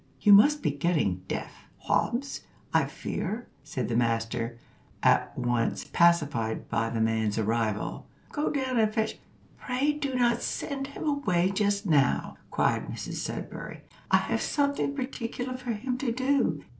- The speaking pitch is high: Yes, high, 205 Hz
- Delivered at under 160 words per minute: Yes, average, 150 wpm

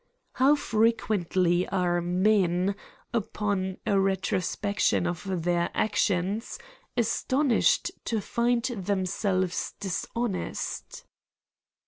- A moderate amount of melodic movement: Yes, average, 3.4 semitones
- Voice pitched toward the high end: Yes, high, 195 Hz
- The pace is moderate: No, slow, 75 wpm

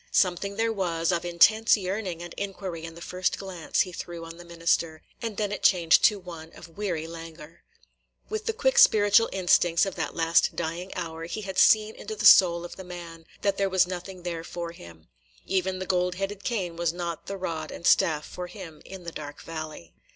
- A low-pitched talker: No, medium, 175 Hz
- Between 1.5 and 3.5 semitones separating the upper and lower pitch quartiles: Yes, average, 2.8 semitones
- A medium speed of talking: No, fast, 210 wpm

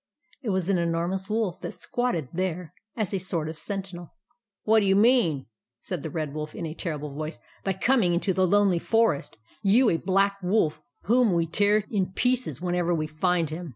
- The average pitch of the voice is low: No, medium, 185 Hz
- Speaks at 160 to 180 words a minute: No, average, 200 wpm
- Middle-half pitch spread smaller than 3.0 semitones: No, average, 3.8 semitones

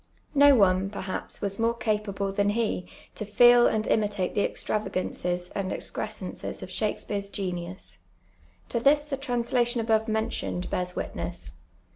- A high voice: Yes, high, 210 Hz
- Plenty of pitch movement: No, average, 3.7 semitones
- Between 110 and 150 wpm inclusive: Yes, average, 140 wpm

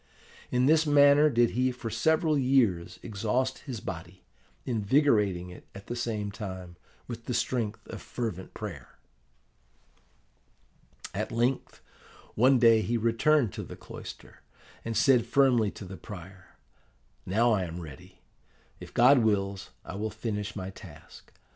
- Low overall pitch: Yes, low, 115 Hz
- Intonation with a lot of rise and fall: No, average, 4.4 semitones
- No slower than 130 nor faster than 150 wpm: Yes, average, 140 wpm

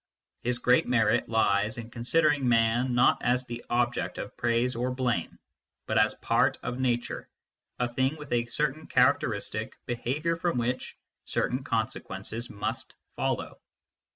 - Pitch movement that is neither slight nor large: No, narrow, 1.8 semitones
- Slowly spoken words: No, average, 145 wpm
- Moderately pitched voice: No, low, 120 Hz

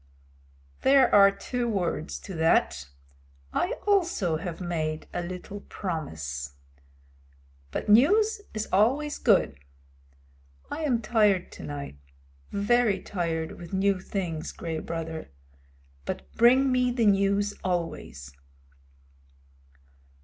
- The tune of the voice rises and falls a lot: Yes, wide, 6.4 semitones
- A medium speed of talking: No, slow, 105 wpm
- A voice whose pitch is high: Yes, high, 195 Hz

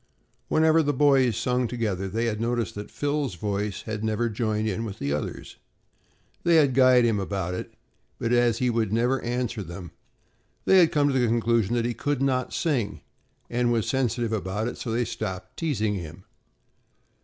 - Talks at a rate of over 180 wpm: Yes, average, 190 wpm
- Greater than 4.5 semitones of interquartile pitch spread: No, average, 3.4 semitones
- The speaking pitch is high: No, low, 115 Hz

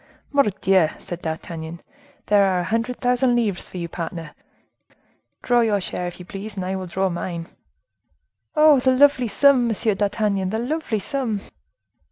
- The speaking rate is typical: Yes, average, 160 wpm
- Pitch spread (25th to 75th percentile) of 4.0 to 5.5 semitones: Yes, average, 5.1 semitones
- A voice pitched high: Yes, high, 205 Hz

